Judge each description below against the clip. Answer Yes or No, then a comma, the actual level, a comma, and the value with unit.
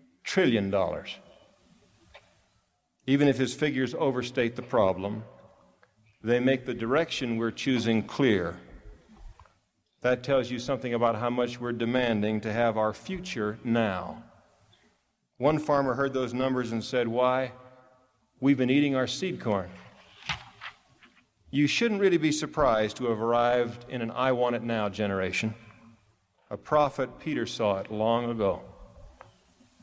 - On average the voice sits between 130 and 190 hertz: No, low, 120 Hz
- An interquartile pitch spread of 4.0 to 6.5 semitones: No, average, 2.7 semitones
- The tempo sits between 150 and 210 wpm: No, slow, 135 wpm